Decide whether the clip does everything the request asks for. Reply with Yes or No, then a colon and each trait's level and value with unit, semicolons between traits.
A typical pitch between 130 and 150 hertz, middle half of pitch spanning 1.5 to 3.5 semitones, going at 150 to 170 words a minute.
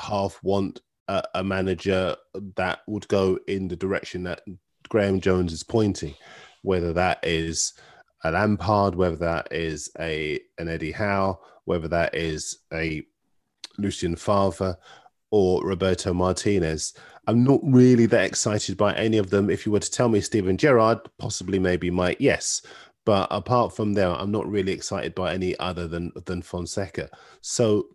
No: very low, 95 Hz; average, 2.9 semitones; average, 155 wpm